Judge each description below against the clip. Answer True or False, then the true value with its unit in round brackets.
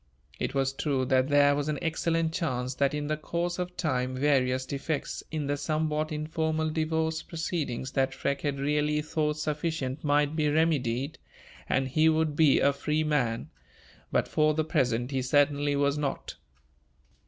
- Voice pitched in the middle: True (150 Hz)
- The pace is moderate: True (165 wpm)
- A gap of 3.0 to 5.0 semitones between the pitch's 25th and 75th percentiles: False (2.5 semitones)